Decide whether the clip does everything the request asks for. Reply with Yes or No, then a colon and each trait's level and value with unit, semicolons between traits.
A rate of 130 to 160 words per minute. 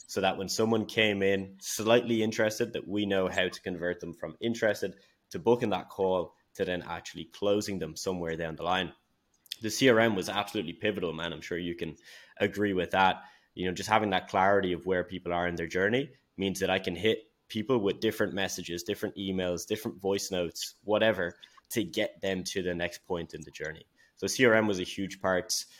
No: average, 200 wpm